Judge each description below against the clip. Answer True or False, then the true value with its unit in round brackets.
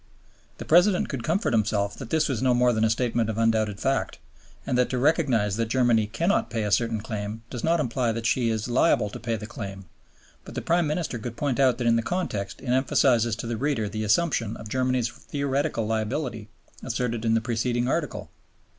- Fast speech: True (210 wpm)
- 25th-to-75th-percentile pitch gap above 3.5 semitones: False (3.2 semitones)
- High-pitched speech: False (120 Hz)